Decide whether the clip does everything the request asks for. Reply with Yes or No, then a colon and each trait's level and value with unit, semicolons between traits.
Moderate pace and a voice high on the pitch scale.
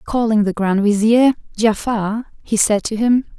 Yes: average, 160 wpm; high, 220 Hz